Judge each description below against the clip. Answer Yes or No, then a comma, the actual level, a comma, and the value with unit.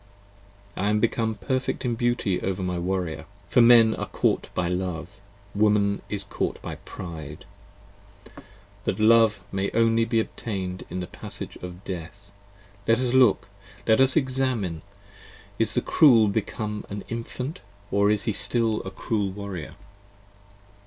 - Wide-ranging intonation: No, average, 3.3 semitones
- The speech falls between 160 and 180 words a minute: No, average, 145 wpm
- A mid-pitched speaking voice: No, low, 105 Hz